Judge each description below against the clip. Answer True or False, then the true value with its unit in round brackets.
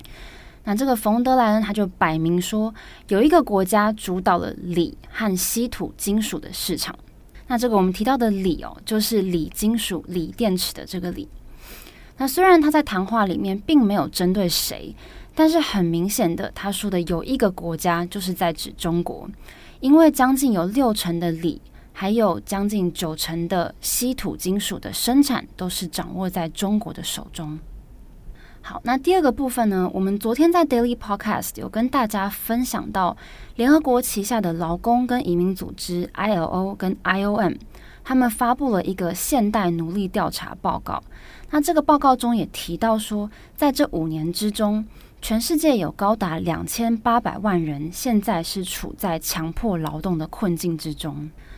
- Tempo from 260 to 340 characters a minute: True (265 characters per minute)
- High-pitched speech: True (200 Hz)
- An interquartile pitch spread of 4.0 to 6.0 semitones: True (5.2 semitones)